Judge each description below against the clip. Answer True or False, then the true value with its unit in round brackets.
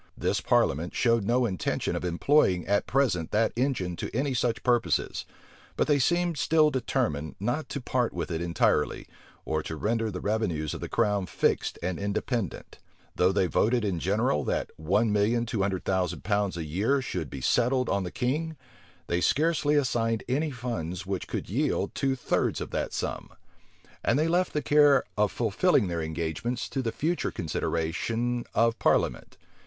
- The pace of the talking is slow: False (170 wpm)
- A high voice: False (115 Hz)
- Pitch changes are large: True (6.1 semitones)